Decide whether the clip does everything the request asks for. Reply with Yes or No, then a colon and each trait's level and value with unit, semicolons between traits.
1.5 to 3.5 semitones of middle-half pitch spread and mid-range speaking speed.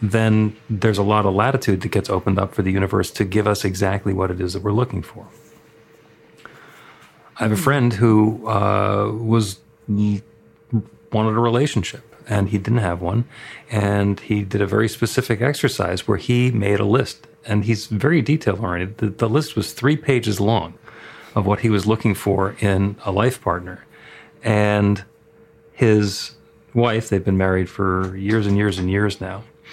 Yes: narrow, 2.5 semitones; average, 175 wpm